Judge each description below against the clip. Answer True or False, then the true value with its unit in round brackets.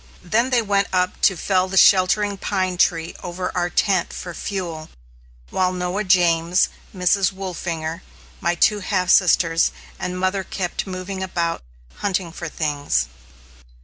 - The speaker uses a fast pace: False (140 wpm)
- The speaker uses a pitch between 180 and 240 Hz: True (185 Hz)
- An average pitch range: False (2.0 semitones)